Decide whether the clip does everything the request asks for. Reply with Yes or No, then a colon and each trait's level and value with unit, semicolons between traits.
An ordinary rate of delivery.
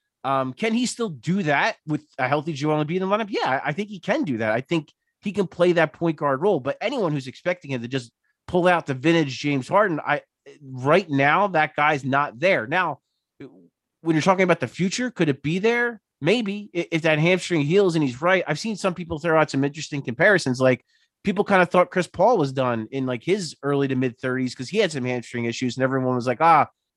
No: fast, 240 wpm